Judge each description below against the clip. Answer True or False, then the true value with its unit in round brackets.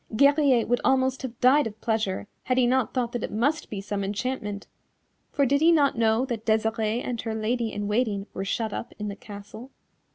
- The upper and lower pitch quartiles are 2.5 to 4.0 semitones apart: True (3.5 semitones)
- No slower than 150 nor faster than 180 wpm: False (205 wpm)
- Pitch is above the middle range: True (230 Hz)